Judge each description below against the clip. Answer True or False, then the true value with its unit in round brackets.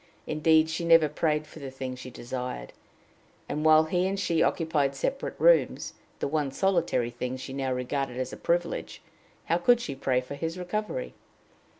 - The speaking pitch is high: False (155 Hz)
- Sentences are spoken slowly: False (175 wpm)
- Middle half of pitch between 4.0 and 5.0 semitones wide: True (4.4 semitones)